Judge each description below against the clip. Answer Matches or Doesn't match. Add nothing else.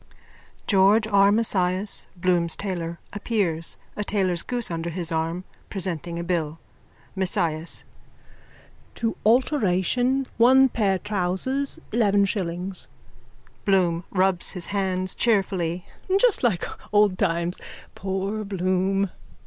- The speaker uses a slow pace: Matches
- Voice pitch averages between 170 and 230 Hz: Matches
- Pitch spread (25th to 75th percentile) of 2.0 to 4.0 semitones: Matches